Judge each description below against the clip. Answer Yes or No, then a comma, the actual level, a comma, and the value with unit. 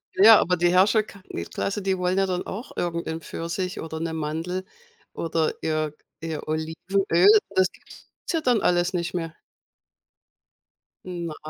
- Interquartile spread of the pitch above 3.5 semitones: No, narrow, 2.6 semitones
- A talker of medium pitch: Yes, medium, 175 Hz